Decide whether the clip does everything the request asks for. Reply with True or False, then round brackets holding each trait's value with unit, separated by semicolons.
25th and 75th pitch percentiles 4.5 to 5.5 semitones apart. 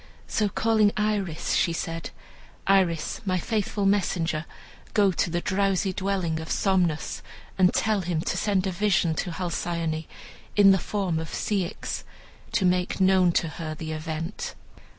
False (3.0 semitones)